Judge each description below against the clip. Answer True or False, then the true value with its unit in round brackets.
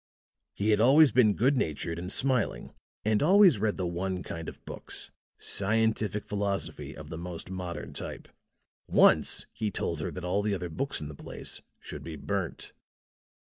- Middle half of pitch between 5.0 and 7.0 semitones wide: False (4.4 semitones)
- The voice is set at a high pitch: False (100 Hz)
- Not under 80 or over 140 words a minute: False (170 wpm)